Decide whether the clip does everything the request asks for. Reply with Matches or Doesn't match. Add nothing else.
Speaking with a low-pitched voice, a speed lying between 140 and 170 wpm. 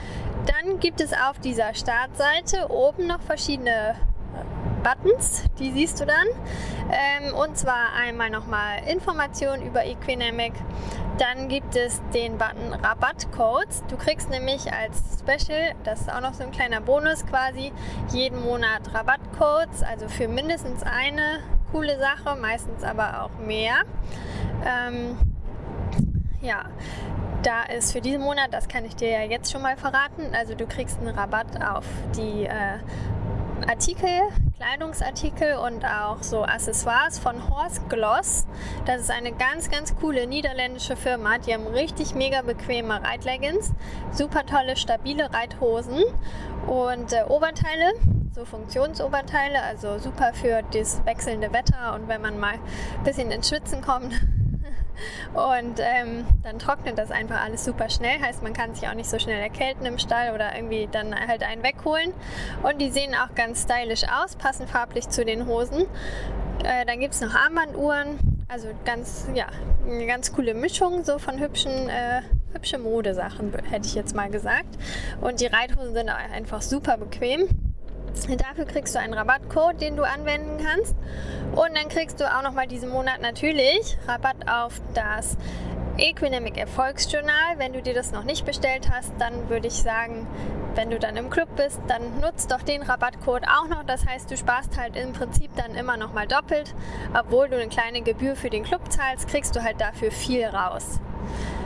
Doesn't match